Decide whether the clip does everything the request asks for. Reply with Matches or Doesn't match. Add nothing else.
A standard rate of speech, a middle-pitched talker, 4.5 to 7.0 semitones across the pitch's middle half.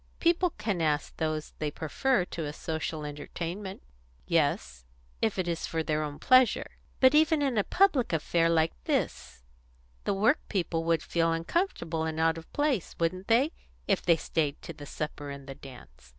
Matches